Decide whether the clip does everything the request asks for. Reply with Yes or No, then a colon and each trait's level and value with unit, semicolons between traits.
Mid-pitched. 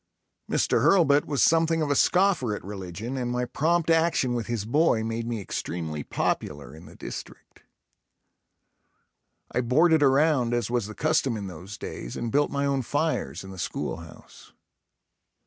No: low, 125 Hz